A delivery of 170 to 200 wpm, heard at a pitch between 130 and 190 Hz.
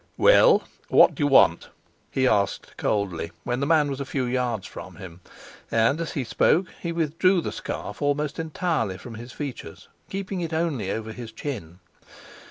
Yes: average, 175 wpm; low, 135 Hz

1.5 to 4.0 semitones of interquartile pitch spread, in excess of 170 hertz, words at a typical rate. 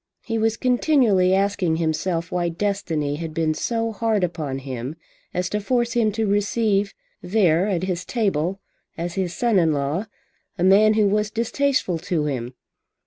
No: average, 4.8 semitones; high, 190 Hz; average, 160 wpm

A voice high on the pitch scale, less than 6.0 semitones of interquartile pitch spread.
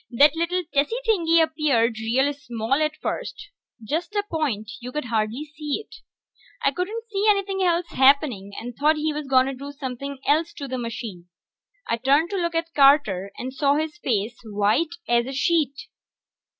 Yes: very high, 280 Hz; average, 5.2 semitones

